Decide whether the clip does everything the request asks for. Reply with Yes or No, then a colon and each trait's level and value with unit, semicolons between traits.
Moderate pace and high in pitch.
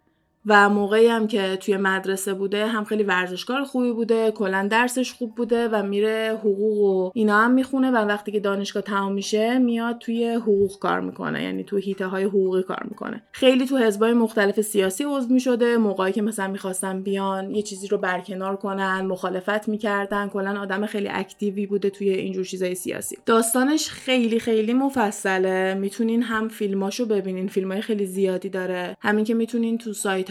No: fast, 170 wpm; high, 205 Hz